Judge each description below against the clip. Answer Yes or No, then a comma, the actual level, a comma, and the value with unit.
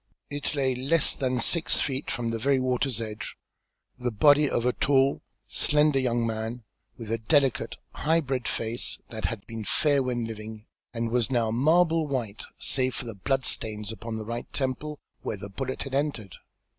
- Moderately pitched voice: No, low, 125 Hz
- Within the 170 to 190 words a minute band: Yes, average, 180 wpm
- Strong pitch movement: No, average, 3.6 semitones